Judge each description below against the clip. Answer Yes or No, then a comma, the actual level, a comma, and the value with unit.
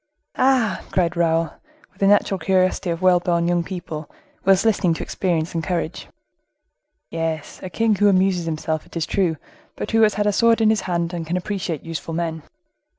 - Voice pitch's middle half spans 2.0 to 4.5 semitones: Yes, average, 3.0 semitones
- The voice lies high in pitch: No, medium, 175 Hz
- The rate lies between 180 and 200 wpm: Yes, average, 190 wpm